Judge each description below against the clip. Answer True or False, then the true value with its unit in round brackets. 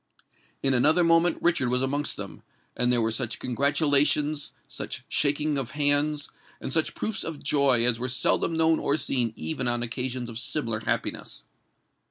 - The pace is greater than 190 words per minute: False (155 wpm)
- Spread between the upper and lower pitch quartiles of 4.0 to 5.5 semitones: False (3.6 semitones)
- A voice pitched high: False (140 Hz)